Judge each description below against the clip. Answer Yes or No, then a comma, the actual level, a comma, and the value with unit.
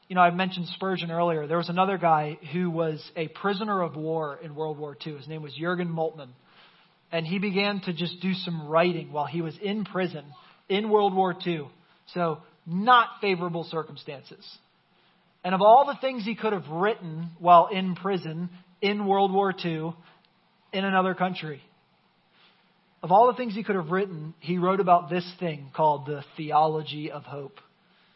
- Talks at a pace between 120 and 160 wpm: No, average, 175 wpm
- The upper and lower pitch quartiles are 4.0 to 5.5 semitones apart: No, average, 3.2 semitones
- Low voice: No, medium, 175 Hz